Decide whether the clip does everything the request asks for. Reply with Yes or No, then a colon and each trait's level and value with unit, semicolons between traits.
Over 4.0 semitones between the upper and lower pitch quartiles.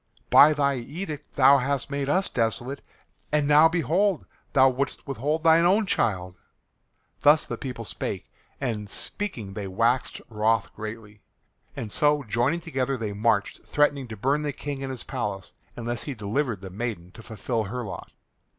Yes: average, 5.0 semitones